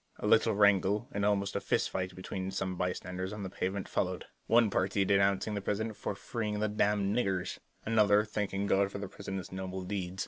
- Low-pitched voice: Yes, low, 100 Hz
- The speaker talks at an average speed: Yes, average, 195 wpm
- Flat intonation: Yes, narrow, 1.7 semitones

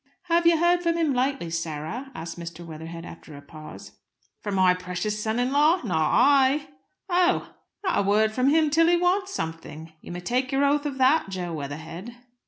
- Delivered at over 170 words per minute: Yes, average, 190 wpm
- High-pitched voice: Yes, high, 240 Hz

